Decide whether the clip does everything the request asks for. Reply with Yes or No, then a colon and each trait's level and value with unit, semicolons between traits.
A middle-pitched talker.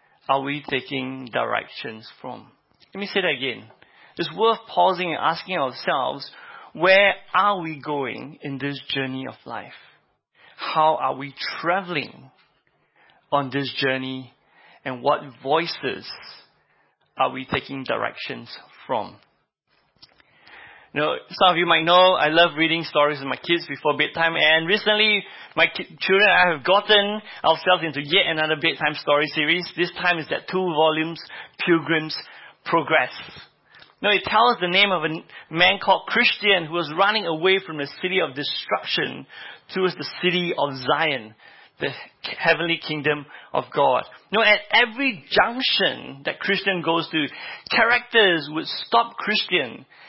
Yes: medium, 165 Hz